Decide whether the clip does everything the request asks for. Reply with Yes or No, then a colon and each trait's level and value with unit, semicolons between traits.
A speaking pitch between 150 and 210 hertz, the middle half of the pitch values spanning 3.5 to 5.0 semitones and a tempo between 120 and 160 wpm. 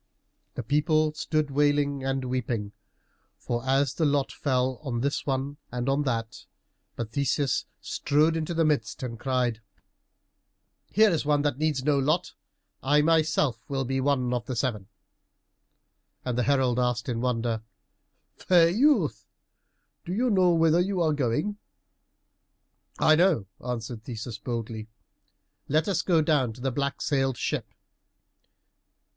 No: medium, 140 Hz; average, 3.8 semitones; average, 140 wpm